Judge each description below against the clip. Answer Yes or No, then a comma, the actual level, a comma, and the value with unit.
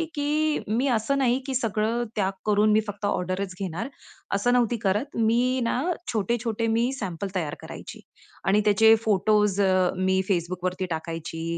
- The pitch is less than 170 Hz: No, high, 210 Hz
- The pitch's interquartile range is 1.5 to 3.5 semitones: No, average, 4.0 semitones